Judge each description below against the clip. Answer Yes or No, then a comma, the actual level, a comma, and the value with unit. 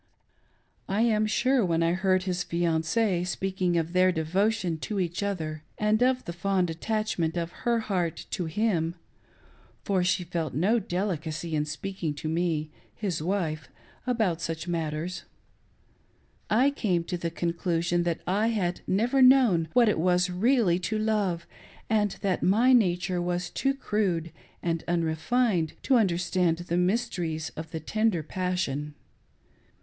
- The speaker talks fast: No, average, 150 wpm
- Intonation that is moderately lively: Yes, average, 4.2 semitones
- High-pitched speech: No, medium, 180 Hz